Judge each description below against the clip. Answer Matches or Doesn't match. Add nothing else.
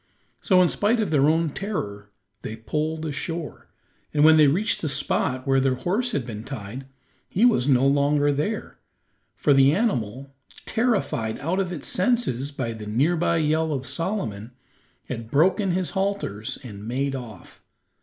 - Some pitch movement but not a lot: Doesn't match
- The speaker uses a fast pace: Doesn't match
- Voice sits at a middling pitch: Matches